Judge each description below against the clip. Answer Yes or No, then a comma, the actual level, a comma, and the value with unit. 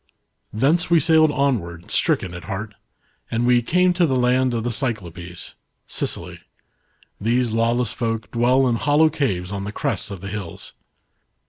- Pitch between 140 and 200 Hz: No, low, 120 Hz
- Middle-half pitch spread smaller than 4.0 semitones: No, average, 4.7 semitones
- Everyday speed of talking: Yes, average, 155 wpm